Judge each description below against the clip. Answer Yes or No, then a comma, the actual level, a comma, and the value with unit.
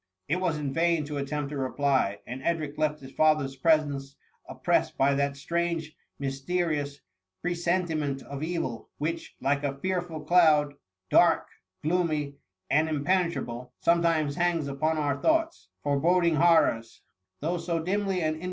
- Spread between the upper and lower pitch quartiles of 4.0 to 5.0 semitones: No, average, 3.3 semitones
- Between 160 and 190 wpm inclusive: No, average, 145 wpm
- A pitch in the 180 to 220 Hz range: No, medium, 155 Hz